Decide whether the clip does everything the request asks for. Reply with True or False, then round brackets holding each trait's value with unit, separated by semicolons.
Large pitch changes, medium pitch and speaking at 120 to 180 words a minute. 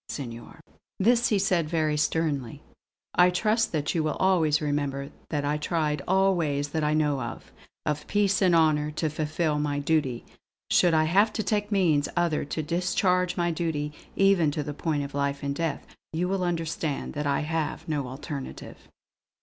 False (3.3 semitones; 155 Hz; 175 wpm)